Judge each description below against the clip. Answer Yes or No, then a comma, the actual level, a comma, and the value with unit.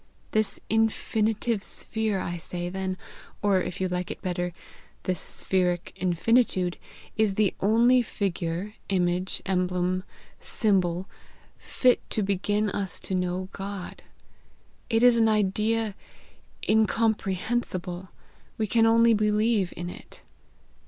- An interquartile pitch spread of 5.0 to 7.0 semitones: No, average, 3.3 semitones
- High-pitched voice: Yes, high, 195 Hz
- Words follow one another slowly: Yes, slow, 115 wpm